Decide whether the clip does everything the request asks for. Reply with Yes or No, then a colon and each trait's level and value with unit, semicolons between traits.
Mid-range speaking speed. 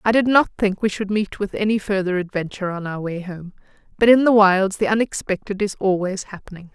No: fast, 215 wpm